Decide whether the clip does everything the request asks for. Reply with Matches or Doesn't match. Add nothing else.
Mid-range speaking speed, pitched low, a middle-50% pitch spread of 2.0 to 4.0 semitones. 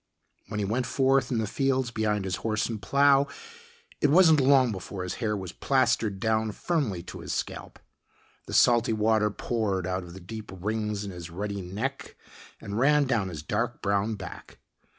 Doesn't match